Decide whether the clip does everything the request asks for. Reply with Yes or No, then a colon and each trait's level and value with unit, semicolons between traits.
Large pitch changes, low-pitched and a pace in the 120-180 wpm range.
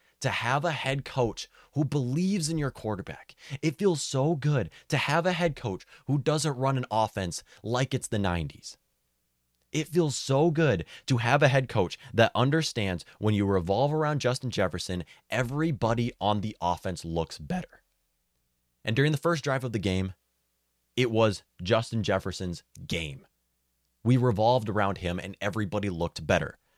Yes: wide, 7.6 semitones; low, 115 Hz; average, 160 wpm